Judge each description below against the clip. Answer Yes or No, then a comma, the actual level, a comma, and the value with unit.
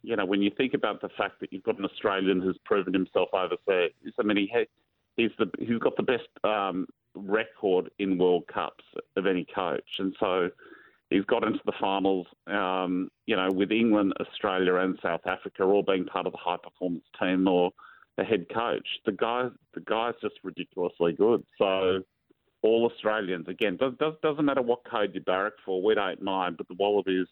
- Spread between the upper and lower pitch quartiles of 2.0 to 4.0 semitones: Yes, average, 3.2 semitones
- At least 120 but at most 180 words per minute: No, average, 195 wpm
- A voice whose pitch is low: Yes, very low, 95 Hz